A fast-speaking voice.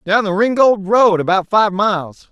No: average, 180 wpm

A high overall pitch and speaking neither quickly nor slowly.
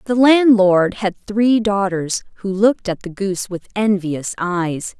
Yes: high, 195 Hz; average, 155 wpm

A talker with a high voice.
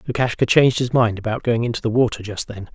No: low, 115 Hz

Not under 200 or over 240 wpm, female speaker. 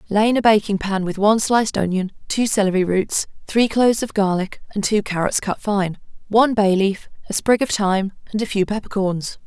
Yes: fast, 205 wpm; female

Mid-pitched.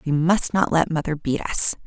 Yes: medium, 160 Hz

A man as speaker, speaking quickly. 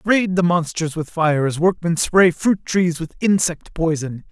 No: male; average, 195 wpm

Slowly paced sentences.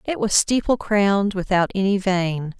No: average, 160 wpm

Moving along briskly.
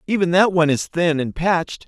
Yes: fast, 225 wpm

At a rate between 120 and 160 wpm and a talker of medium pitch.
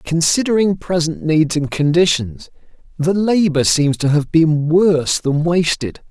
Yes: average, 140 wpm; medium, 160 Hz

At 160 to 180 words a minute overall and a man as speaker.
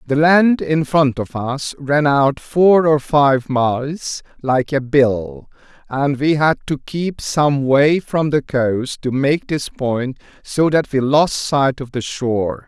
Yes: average, 175 wpm; male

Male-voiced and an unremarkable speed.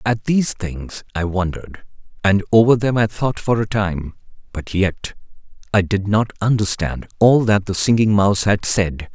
Yes: male; average, 170 wpm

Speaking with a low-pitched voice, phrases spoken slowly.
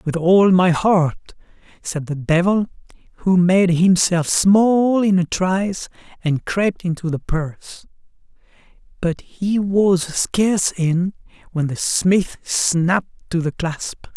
No: medium, 180 Hz; slow, 130 wpm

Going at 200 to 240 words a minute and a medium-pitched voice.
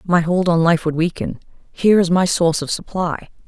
Yes: fast, 205 wpm; medium, 170 Hz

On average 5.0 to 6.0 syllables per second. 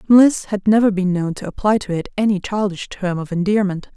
Yes: 5.5 syllables/s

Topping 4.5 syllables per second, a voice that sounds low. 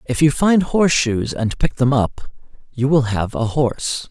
No: 4.4 syllables/s; low, 130 Hz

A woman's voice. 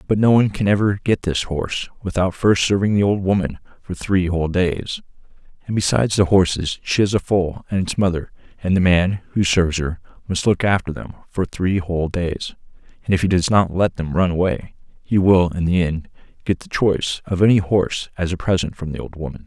No: male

